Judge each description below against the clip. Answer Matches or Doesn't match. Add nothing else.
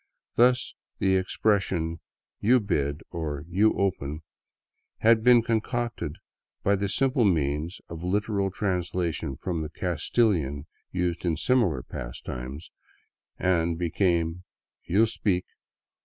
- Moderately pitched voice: Doesn't match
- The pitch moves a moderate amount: Matches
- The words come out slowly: Matches